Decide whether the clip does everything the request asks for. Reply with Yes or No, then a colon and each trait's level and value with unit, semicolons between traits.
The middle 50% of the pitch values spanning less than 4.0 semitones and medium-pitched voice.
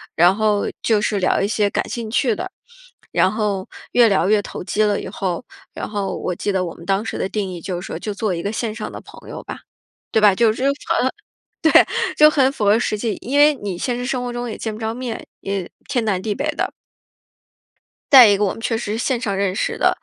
No: average, 3.3 semitones; high, 215 Hz